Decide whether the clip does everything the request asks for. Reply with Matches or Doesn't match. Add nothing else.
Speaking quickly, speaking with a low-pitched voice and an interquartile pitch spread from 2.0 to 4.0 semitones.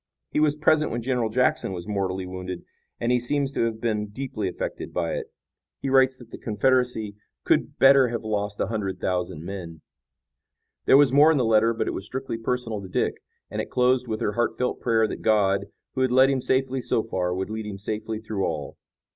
Doesn't match